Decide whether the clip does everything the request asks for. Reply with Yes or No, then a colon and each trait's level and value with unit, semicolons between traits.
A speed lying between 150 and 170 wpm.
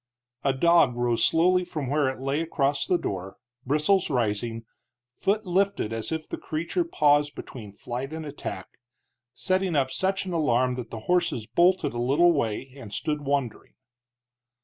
Yes: average, 160 wpm